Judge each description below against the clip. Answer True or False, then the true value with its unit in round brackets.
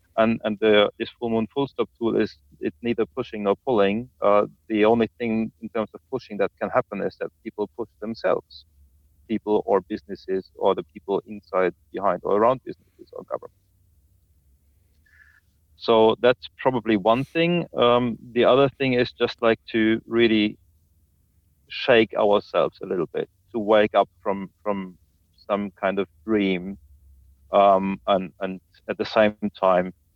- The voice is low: True (105 Hz)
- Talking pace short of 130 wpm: False (155 wpm)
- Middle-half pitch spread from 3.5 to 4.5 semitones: True (4.2 semitones)